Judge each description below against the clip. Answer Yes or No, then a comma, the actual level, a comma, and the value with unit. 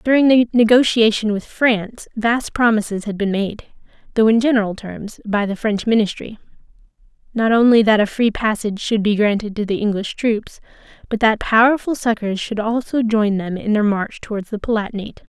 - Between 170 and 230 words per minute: Yes, average, 175 wpm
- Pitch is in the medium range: No, high, 215 Hz